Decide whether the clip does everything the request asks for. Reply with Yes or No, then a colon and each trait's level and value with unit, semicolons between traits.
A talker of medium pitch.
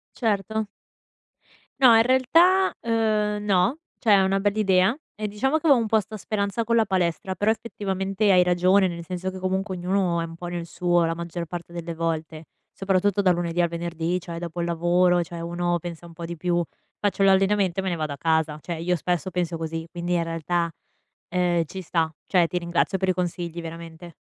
Yes: medium, 180 Hz